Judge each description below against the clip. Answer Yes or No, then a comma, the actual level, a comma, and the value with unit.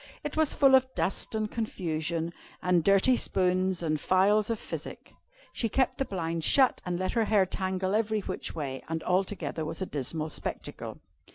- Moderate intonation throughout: Yes, average, 4.6 semitones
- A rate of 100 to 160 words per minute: No, average, 175 wpm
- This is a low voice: No, medium, 185 Hz